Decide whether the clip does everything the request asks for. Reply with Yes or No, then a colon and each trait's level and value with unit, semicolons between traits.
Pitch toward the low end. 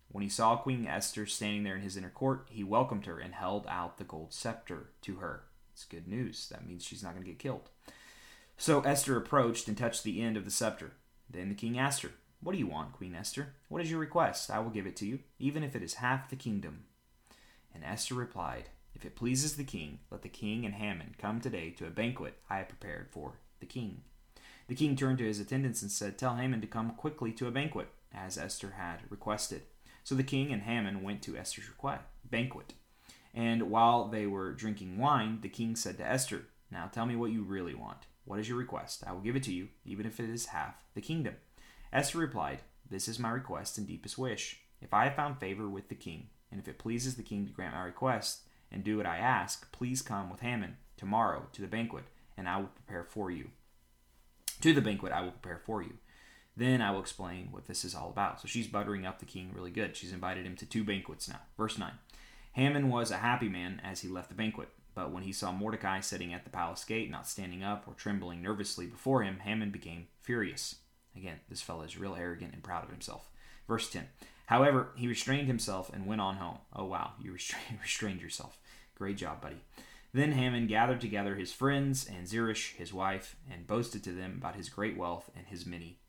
Yes: low, 105 Hz